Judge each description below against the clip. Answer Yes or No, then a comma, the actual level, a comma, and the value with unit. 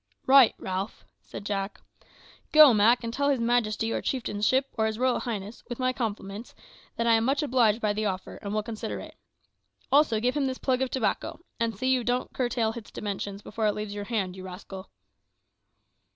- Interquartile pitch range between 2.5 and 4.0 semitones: Yes, average, 3.5 semitones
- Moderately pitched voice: No, high, 225 Hz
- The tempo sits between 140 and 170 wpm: No, average, 195 wpm